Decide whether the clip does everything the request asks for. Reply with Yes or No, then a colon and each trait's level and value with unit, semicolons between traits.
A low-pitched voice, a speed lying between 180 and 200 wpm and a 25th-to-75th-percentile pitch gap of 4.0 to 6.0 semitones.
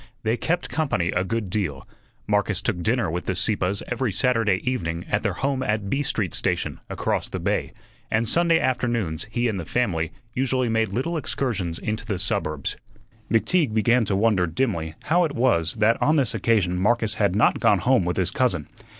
Yes: low, 110 Hz; average, 185 wpm; average, 5.3 semitones